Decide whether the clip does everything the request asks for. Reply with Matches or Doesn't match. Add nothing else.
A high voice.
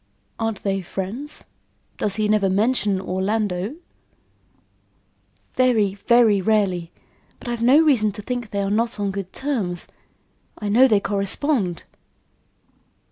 Matches